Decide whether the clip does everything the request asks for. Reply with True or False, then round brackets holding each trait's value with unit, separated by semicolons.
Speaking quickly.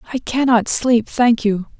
False (165 wpm)